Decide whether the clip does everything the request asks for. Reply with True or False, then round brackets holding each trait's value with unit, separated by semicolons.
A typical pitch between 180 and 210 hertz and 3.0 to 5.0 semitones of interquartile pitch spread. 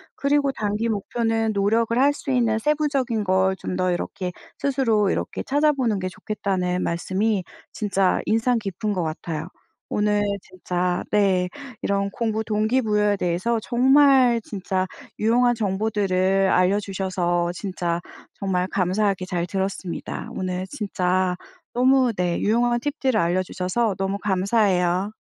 True (200 Hz; 3.8 semitones)